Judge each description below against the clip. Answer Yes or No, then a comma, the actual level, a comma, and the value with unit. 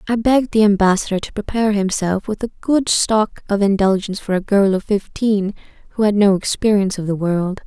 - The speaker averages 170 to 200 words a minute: Yes, average, 195 wpm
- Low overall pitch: No, high, 205 Hz